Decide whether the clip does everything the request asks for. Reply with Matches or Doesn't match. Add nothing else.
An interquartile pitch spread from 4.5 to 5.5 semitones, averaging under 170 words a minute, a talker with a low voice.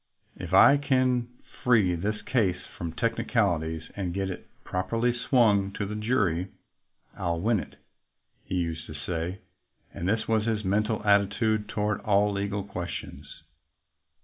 Doesn't match